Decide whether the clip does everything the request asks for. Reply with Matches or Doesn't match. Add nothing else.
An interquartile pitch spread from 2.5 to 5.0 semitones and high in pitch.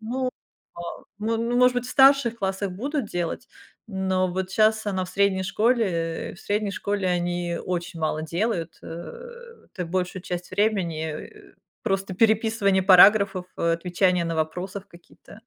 Matches